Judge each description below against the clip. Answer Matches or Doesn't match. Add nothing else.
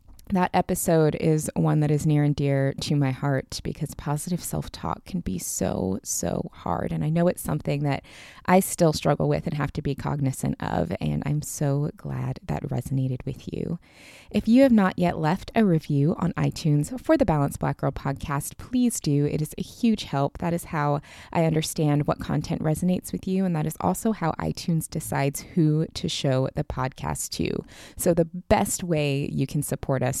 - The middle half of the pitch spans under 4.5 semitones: Matches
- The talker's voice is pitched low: Doesn't match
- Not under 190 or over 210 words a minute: Matches